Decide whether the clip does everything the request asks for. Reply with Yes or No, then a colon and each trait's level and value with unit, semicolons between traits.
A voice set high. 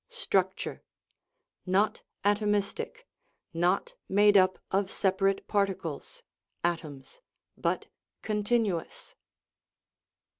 Yes: high, 195 Hz